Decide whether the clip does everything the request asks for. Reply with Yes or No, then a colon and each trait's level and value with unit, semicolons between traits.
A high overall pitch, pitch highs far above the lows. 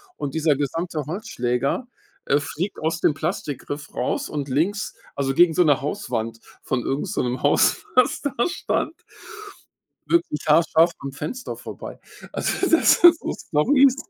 No: medium, 155 Hz; wide, 6.1 semitones